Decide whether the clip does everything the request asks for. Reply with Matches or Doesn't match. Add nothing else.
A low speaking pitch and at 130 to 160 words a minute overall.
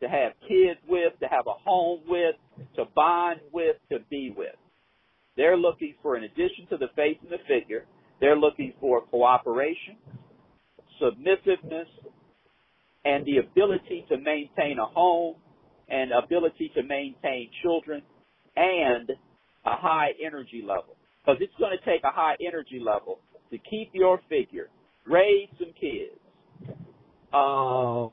Doesn't match